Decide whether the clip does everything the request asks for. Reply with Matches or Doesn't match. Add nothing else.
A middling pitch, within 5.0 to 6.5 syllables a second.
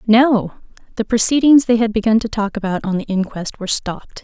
Doesn't match